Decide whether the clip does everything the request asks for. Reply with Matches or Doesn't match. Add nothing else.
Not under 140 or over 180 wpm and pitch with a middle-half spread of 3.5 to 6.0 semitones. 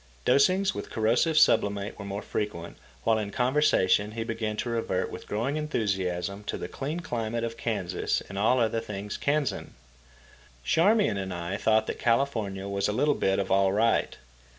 Matches